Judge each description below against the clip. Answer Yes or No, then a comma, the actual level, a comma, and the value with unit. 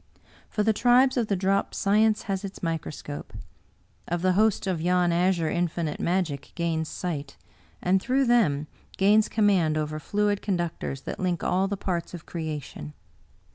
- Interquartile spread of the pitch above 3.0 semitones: Yes, average, 3.9 semitones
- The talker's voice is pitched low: No, medium, 180 Hz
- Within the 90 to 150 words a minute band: No, average, 165 wpm